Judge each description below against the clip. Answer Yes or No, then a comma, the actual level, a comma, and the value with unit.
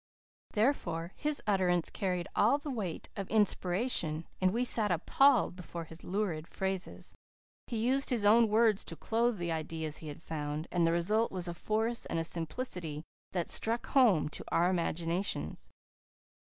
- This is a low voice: No, medium, 185 Hz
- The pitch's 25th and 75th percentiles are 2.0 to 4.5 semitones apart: No, average, 5.1 semitones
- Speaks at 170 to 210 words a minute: No, average, 155 wpm